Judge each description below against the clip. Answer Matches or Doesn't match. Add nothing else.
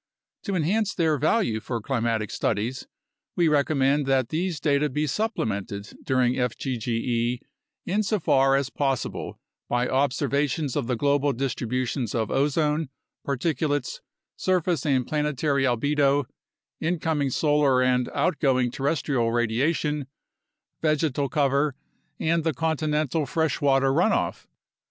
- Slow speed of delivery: Matches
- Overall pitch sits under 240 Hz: Matches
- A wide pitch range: Doesn't match